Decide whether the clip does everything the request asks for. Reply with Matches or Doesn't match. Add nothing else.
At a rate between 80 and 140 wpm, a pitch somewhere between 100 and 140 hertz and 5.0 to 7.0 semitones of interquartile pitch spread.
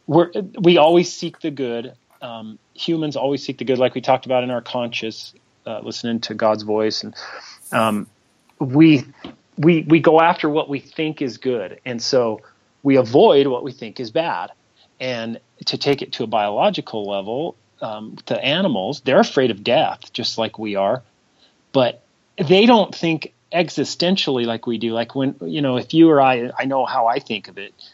Doesn't match